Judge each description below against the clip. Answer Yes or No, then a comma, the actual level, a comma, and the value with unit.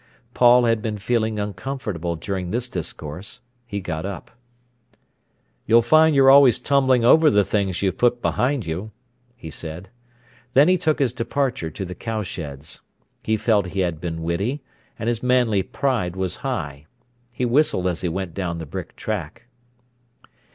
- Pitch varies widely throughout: Yes, wide, 5.8 semitones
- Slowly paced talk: No, average, 160 wpm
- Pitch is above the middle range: No, low, 105 Hz